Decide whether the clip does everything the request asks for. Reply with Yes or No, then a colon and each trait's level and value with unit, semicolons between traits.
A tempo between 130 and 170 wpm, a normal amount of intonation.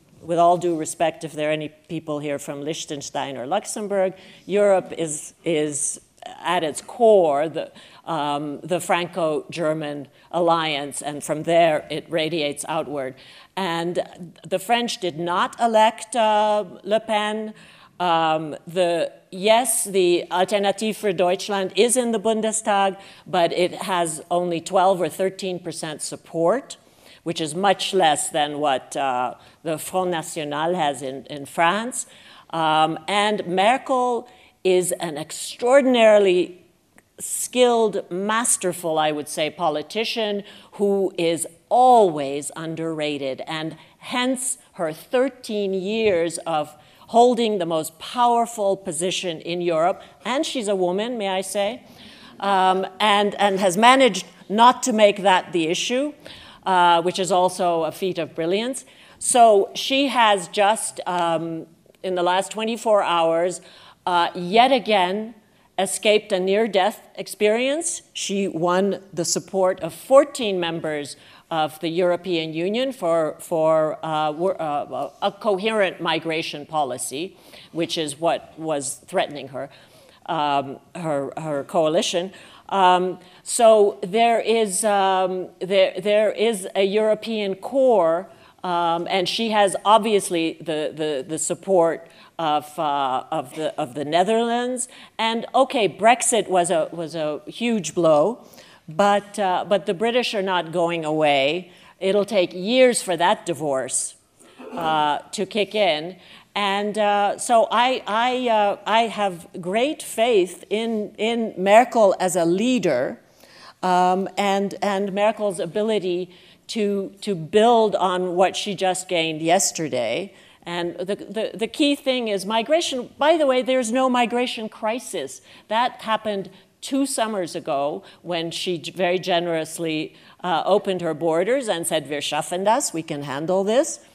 Yes: slow, 135 wpm; average, 4.6 semitones